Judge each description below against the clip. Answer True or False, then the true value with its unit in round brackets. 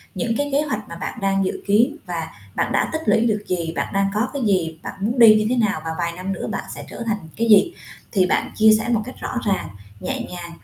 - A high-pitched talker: True (210 Hz)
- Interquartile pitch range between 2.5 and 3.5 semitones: False (4.2 semitones)